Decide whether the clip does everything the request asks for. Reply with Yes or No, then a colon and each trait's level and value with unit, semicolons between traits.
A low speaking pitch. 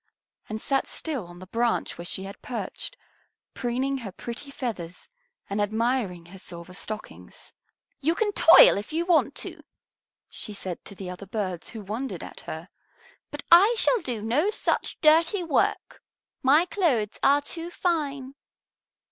No: high, 240 Hz